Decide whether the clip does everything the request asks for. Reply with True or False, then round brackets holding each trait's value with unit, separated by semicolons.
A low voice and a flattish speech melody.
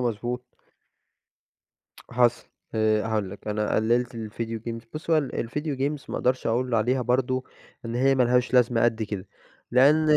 True (120 Hz; 2.3 semitones)